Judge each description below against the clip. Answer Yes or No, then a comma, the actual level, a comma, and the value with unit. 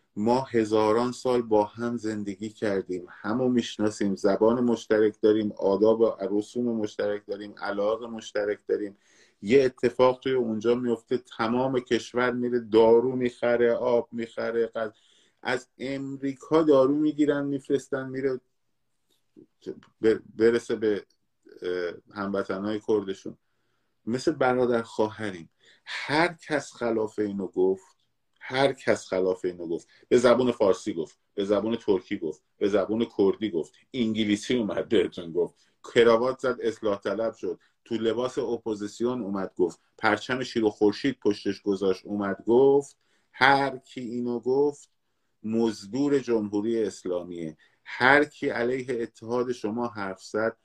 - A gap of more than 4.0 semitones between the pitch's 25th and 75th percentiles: No, average, 3.2 semitones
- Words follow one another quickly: No, average, 125 wpm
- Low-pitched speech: Yes, low, 115 Hz